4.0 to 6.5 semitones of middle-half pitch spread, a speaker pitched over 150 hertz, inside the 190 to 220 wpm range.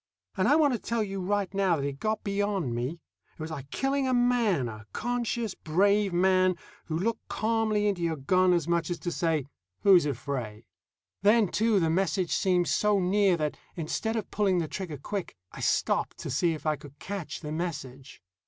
Yes: average, 4.9 semitones; medium, 185 Hz; average, 195 wpm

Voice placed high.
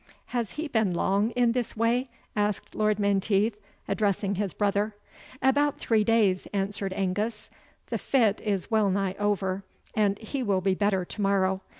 Yes: high, 205 Hz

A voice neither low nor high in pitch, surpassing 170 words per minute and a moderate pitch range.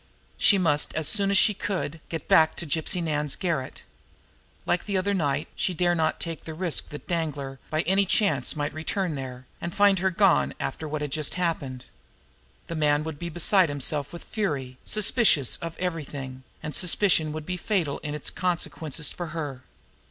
Yes: medium, 160 Hz; average, 180 wpm; average, 3.7 semitones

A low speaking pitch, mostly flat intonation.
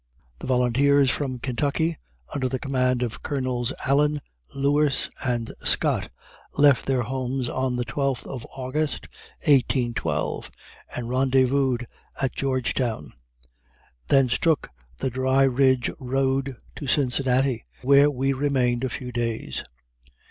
Yes: low, 130 Hz; narrow, 1.9 semitones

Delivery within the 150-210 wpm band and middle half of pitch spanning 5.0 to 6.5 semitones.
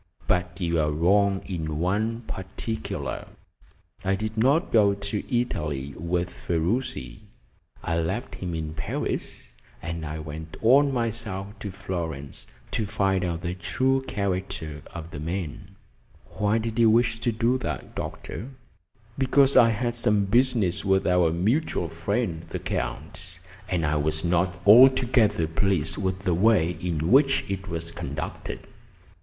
No: average, 140 wpm; average, 5.3 semitones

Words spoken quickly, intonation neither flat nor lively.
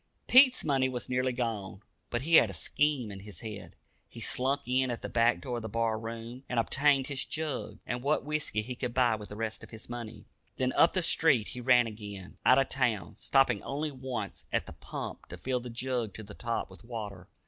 Yes: fast, 225 wpm; average, 3.1 semitones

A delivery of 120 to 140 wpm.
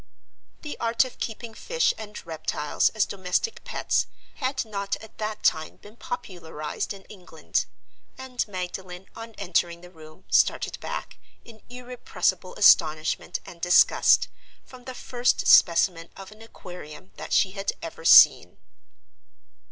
Yes: slow, 135 wpm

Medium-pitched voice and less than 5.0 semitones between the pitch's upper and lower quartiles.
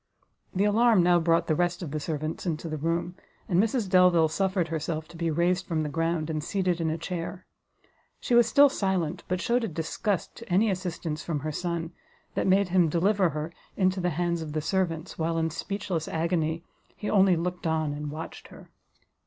Yes: medium, 170 Hz; average, 2.7 semitones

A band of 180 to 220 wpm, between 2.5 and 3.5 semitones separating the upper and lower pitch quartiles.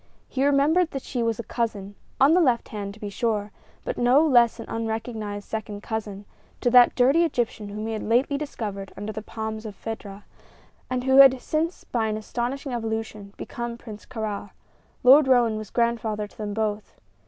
Yes: average, 185 wpm; average, 3.1 semitones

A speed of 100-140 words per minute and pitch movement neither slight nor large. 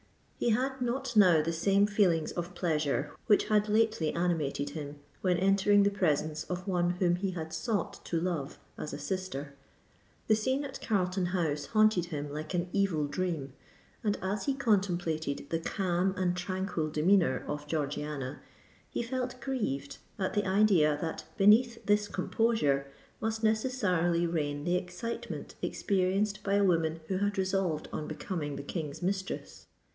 No: average, 155 wpm; average, 4.5 semitones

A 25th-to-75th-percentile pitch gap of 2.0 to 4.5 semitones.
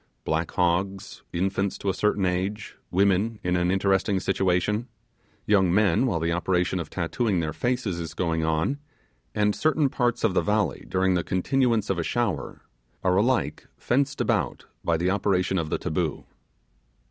Yes: average, 3.2 semitones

